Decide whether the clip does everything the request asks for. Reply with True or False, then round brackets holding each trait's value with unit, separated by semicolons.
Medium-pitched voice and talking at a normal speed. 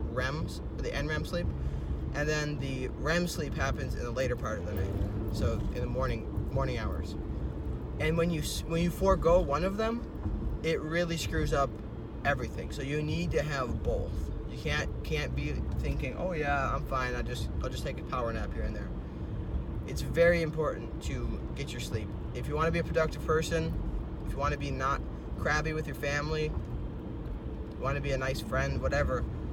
True (145 Hz; 195 wpm)